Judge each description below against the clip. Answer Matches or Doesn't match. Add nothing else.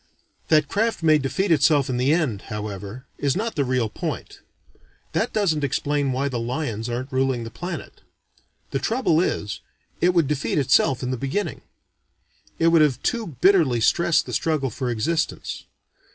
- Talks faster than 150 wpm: Matches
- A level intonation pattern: Doesn't match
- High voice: Doesn't match